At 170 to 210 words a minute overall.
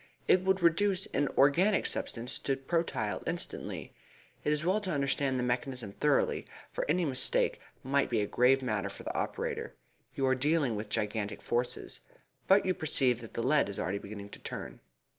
Yes: average, 180 wpm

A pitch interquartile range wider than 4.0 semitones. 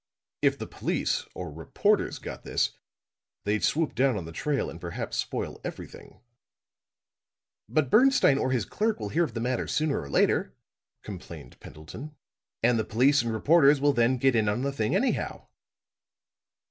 Yes: wide, 5.6 semitones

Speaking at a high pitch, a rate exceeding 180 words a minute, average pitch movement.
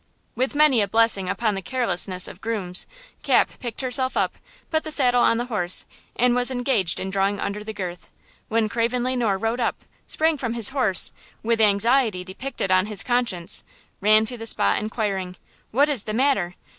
Yes: high, 225 Hz; average, 190 wpm; average, 4.1 semitones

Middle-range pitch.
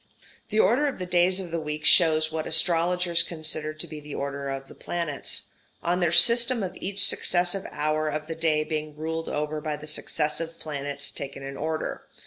Yes: medium, 155 Hz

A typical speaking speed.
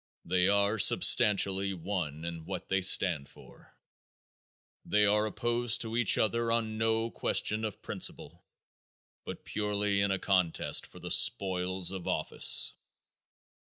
No: slow, 130 wpm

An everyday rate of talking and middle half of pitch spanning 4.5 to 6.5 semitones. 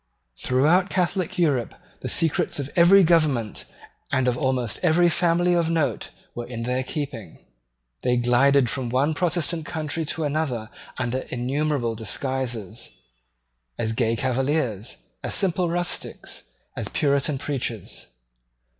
No: slow, 125 wpm; average, 5.1 semitones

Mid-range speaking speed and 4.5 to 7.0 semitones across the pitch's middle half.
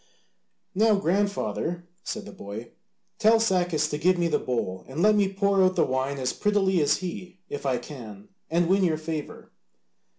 Yes: average, 175 wpm; wide, 5.6 semitones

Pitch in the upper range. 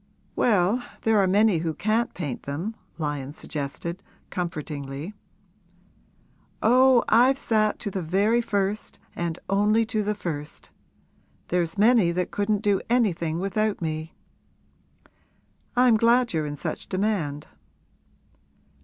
Yes: high, 195 Hz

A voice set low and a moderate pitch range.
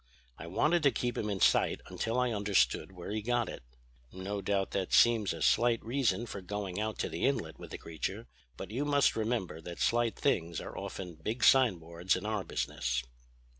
Yes: low, 105 Hz; average, 4.3 semitones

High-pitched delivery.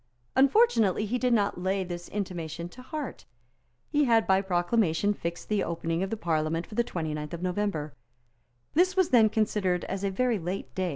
Yes: high, 195 Hz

